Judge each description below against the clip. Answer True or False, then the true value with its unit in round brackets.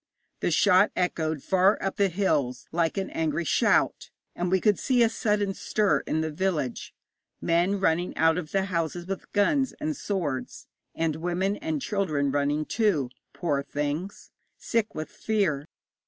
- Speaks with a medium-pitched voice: True (180 Hz)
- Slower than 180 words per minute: True (155 wpm)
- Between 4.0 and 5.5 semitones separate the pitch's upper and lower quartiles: True (4.5 semitones)